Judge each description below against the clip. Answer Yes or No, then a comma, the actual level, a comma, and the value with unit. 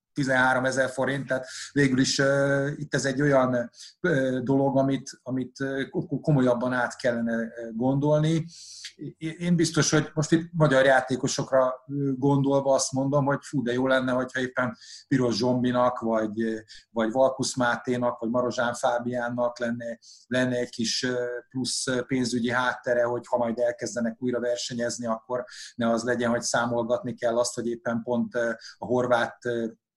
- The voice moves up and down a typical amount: No, narrow, 2.1 semitones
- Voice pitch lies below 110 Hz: No, low, 125 Hz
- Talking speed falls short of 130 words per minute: No, fast, 155 wpm